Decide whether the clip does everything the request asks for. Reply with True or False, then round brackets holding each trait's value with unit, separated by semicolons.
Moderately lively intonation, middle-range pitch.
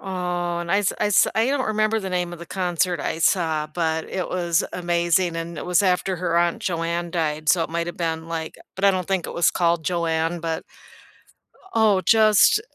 False (2.0 semitones; 175 Hz)